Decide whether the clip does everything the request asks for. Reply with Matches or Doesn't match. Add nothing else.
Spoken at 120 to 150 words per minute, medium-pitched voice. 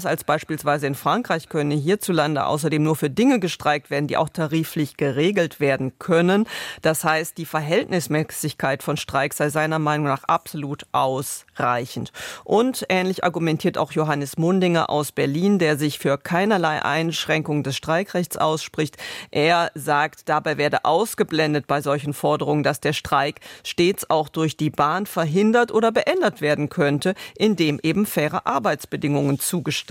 Matches